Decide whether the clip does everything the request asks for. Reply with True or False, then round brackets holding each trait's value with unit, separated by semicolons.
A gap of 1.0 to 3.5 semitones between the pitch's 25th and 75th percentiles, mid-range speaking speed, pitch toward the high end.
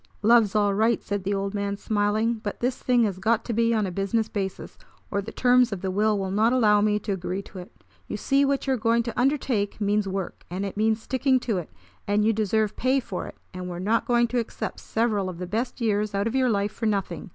False (2.8 semitones; 250 wpm; 210 Hz)